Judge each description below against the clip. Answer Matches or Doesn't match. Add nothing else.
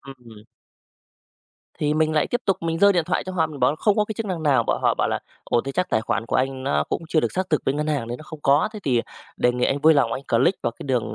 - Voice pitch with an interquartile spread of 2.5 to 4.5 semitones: Doesn't match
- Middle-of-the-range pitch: Matches